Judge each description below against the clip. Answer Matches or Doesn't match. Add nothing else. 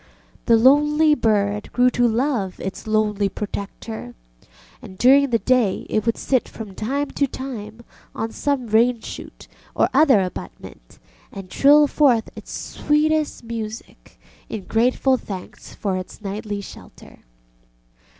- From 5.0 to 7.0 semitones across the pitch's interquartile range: Doesn't match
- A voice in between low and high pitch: Doesn't match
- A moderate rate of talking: Doesn't match